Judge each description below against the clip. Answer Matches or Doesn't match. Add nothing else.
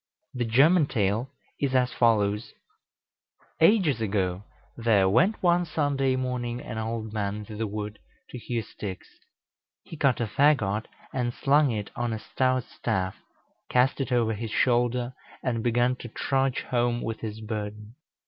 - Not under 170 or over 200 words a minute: Doesn't match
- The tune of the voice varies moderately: Matches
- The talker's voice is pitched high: Doesn't match